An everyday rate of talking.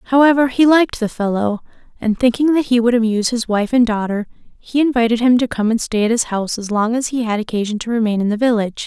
No: fast, 245 wpm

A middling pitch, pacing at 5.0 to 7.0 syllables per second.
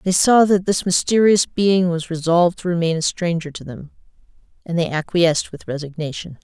Yes: medium, 170 Hz; 5.4 syllables/s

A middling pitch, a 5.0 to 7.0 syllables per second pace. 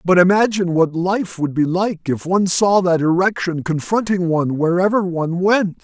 Yes: medium, 180 Hz; 5.1 syllables/s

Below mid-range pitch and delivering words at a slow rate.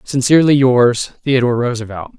Yes: low, 125 Hz; slow, 110 wpm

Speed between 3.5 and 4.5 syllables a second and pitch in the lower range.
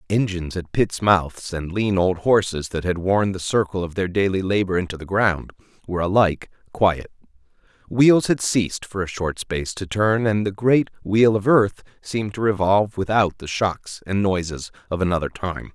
No: 5.0 syllables/s; very low, 95 Hz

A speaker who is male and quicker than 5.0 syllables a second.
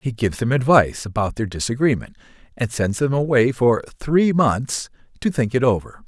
Yes: male; 5.2 syllables/s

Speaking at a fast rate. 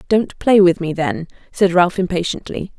No: average, 170 wpm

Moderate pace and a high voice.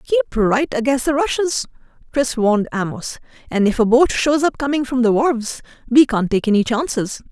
Yes: average, 190 wpm; very high, 250 Hz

